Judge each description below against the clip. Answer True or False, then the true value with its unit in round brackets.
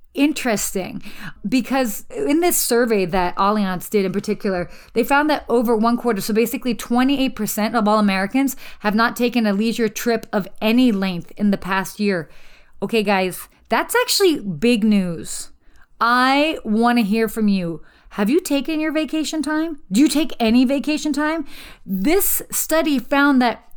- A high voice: True (235 Hz)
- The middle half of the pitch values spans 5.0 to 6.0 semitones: True (5.3 semitones)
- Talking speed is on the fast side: False (160 wpm)